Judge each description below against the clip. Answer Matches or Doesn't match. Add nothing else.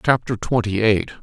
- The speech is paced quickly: Doesn't match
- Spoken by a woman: Doesn't match